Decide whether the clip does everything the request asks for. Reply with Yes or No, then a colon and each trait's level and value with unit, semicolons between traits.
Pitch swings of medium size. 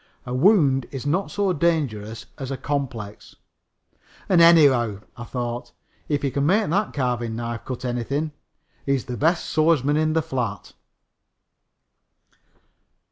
Yes: average, 4.7 semitones